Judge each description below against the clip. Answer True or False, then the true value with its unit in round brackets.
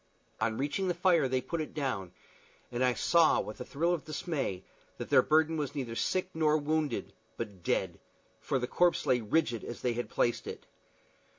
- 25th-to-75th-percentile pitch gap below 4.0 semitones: False (4.9 semitones)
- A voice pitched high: False (145 Hz)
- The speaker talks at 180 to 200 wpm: True (190 wpm)